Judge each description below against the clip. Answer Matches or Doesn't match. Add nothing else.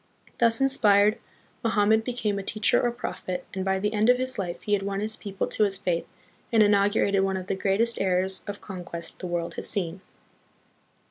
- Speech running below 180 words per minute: Doesn't match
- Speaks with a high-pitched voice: Matches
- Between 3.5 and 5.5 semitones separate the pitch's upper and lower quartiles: Doesn't match